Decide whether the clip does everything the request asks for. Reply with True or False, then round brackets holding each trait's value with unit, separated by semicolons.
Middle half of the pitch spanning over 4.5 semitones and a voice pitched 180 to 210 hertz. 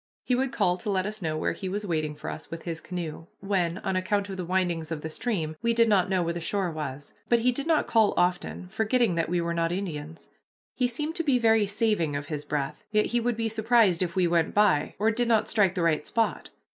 True (5.1 semitones; 185 Hz)